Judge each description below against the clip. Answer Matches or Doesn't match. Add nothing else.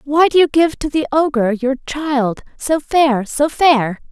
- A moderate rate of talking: Matches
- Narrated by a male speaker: Doesn't match